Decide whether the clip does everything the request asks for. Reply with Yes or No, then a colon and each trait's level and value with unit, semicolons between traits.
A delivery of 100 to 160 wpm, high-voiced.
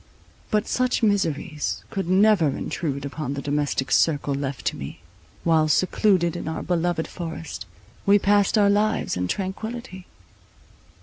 No: slow, 135 wpm; medium, 170 Hz